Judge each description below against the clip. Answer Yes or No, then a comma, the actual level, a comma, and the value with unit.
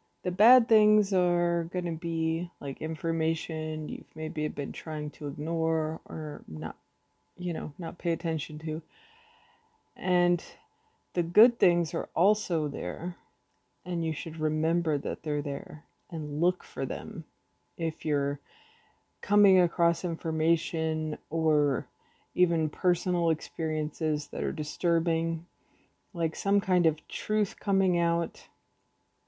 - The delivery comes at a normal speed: No, slow, 125 wpm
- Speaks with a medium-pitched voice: Yes, medium, 165 Hz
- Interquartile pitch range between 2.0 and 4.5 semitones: Yes, narrow, 2.5 semitones